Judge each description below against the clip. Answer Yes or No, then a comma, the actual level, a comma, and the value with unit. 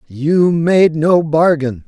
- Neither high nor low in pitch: Yes, medium, 160 Hz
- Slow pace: Yes, slow, 130 wpm